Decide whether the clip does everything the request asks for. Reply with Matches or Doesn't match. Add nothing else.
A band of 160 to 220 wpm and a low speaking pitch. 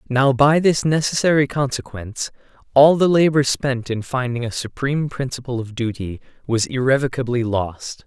Doesn't match